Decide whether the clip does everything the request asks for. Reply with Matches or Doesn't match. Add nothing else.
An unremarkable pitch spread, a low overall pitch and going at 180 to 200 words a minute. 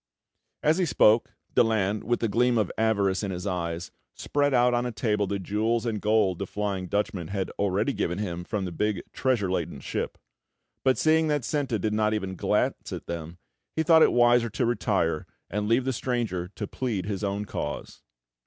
Matches